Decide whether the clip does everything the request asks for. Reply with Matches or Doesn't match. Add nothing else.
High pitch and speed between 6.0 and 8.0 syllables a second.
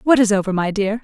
Matches